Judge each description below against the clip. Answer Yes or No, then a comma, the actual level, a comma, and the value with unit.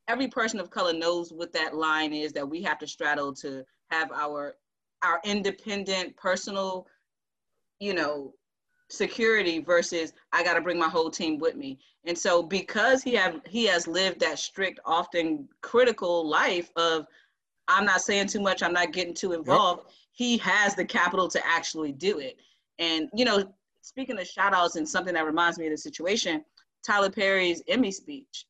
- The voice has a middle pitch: Yes, medium, 180 Hz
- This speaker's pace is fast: No, average, 175 wpm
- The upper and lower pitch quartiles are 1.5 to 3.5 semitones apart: No, average, 3.9 semitones